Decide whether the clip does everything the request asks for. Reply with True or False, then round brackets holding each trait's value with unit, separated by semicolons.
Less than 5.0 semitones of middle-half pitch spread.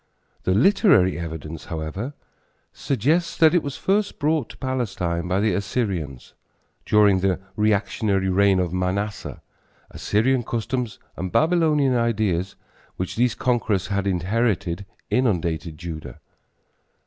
False (5.6 semitones)